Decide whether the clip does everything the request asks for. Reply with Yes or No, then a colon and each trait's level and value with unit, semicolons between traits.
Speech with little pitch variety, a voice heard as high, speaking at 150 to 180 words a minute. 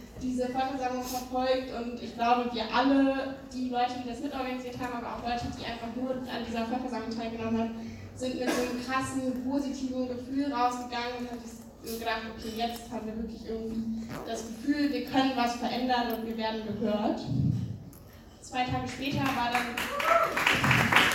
Yes: narrow, 1.9 semitones; high, 245 Hz; average, 165 wpm